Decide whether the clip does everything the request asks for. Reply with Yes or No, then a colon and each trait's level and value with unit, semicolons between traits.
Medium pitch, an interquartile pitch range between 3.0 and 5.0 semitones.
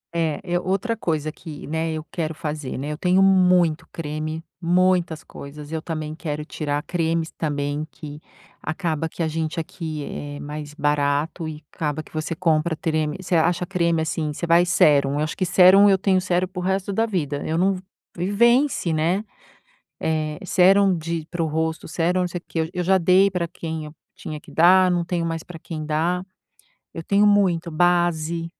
No: medium, 165 Hz; narrow, 2.6 semitones